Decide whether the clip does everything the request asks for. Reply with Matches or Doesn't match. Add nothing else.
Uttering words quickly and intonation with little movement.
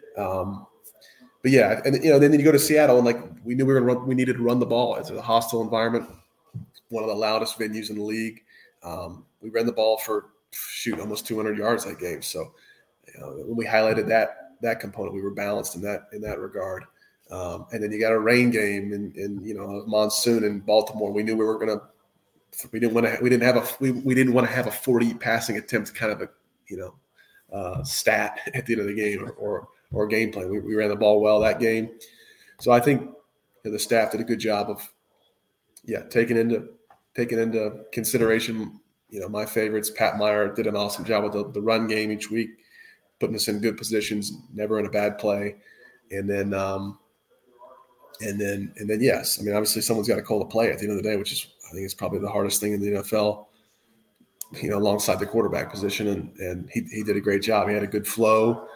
Matches